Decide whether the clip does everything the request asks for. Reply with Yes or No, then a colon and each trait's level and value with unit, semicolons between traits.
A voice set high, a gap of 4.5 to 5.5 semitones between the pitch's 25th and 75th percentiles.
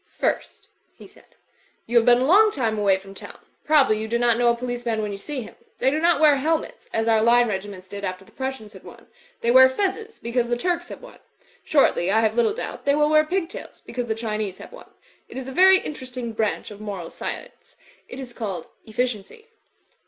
Yes: high, 240 Hz; average, 5.1 semitones